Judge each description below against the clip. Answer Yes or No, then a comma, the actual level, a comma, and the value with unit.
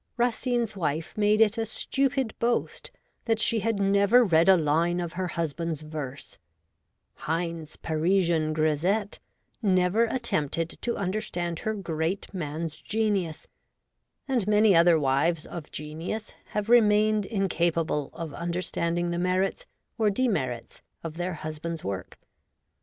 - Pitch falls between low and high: Yes, medium, 175 Hz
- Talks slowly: Yes, slow, 125 wpm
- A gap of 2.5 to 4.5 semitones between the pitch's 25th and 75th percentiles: No, average, 4.9 semitones